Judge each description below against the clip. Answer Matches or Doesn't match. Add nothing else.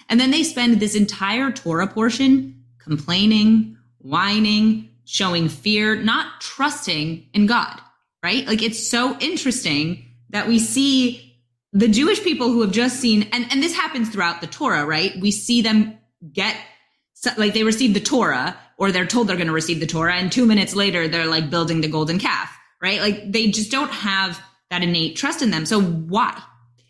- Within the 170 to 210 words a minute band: Matches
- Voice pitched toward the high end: Matches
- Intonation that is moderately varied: Doesn't match